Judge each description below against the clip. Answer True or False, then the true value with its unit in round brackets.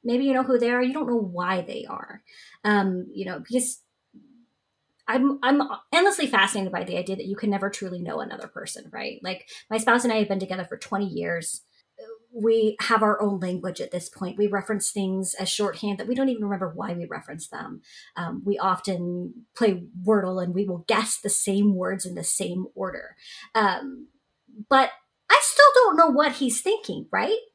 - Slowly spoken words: False (200 wpm)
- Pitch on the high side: True (210 Hz)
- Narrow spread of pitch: False (5.0 semitones)